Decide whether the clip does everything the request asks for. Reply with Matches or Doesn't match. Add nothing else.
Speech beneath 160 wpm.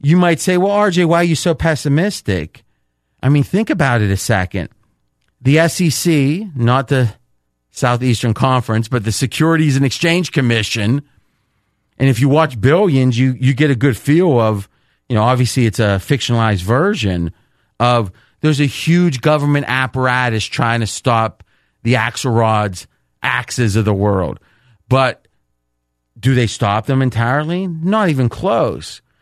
Matches